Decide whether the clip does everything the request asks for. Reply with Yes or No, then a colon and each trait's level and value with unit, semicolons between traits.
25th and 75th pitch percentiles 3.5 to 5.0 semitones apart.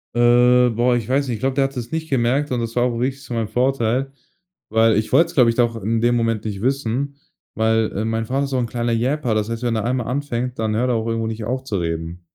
No: narrow, 2.4 semitones